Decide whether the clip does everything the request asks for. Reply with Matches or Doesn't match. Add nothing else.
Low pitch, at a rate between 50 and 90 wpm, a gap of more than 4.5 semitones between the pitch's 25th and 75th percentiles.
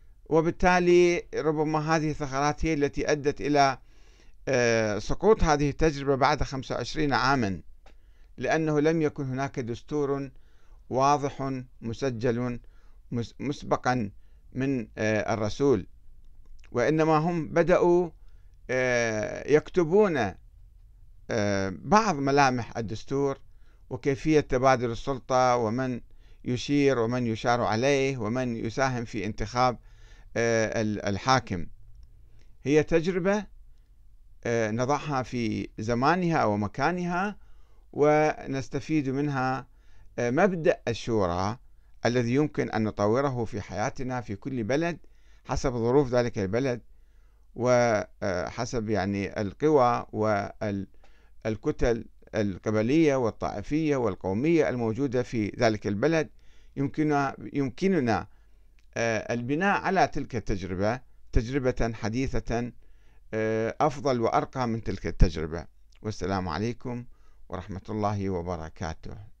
Matches